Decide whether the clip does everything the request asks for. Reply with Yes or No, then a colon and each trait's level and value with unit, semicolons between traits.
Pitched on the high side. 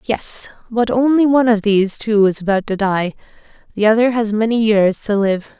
Yes: high, 215 Hz